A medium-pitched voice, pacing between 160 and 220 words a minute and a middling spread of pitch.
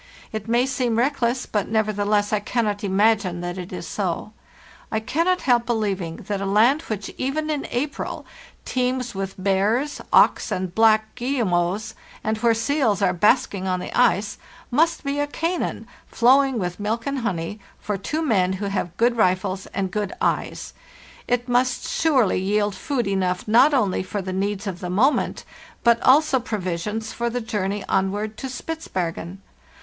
No: high, 215 Hz; average, 165 wpm; average, 4.3 semitones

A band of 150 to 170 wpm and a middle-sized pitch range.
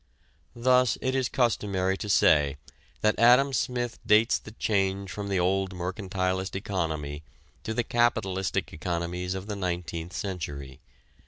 No: slow, 135 wpm; average, 3.8 semitones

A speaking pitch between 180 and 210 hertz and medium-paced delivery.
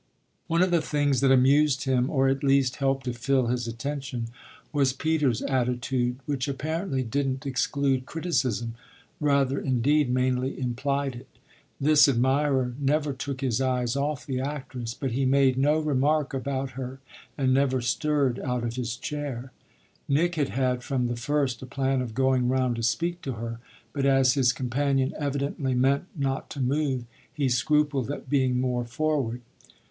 No: low, 135 Hz; average, 165 wpm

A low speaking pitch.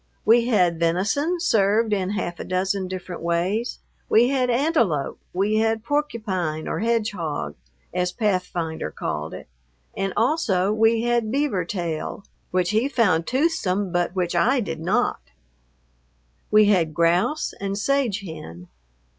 No: high, 200 Hz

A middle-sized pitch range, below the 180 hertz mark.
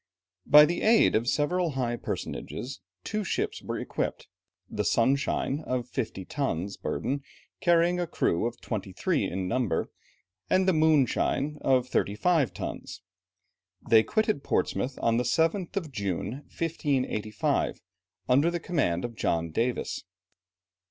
No: wide, 6.4 semitones; low, 135 Hz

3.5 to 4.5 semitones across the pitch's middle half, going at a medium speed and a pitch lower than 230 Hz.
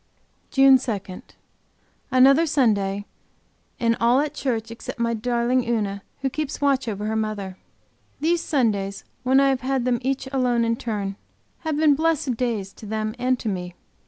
No: average, 3.9 semitones; average, 160 wpm; high, 240 Hz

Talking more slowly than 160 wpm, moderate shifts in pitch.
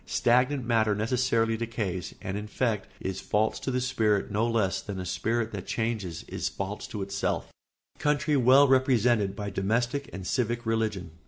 No: average, 170 wpm; average, 3.6 semitones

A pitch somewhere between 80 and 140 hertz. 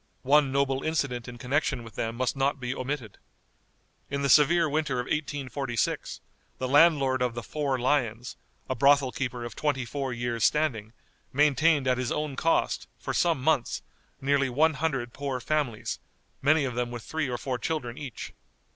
Yes: low, 135 Hz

